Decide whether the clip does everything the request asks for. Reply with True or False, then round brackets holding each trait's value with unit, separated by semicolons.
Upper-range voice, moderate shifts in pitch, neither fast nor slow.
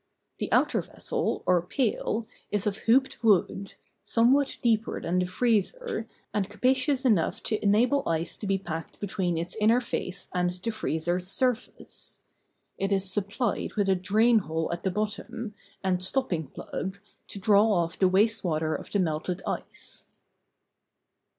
True (200 Hz; 4.0 semitones; 150 wpm)